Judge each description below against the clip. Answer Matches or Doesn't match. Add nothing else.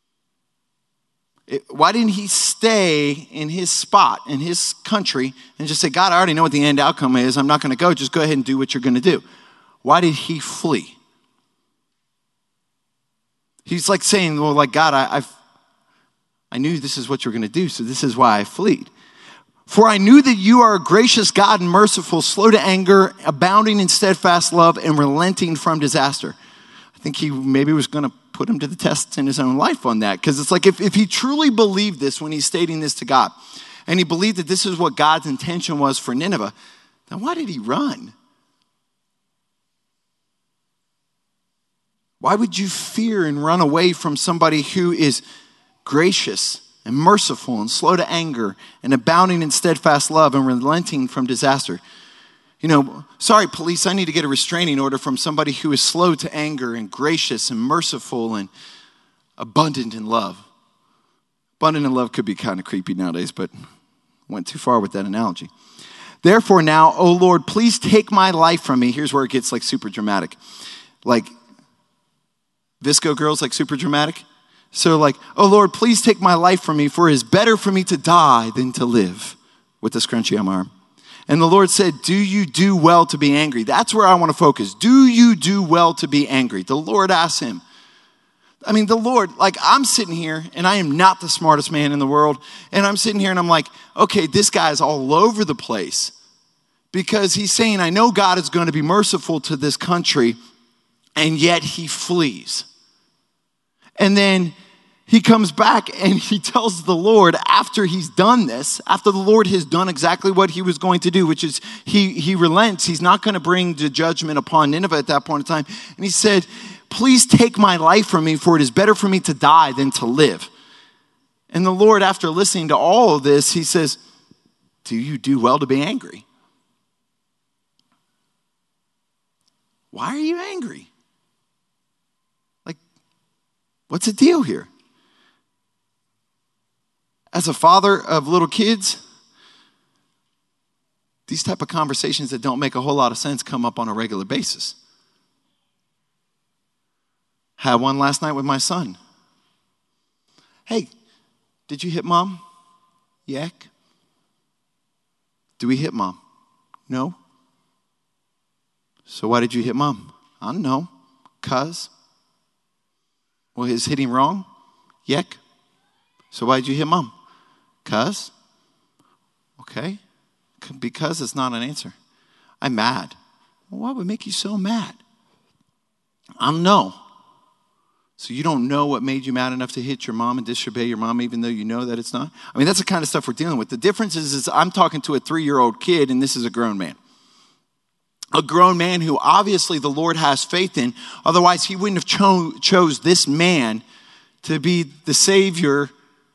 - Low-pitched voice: Doesn't match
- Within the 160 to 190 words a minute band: Matches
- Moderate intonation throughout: Doesn't match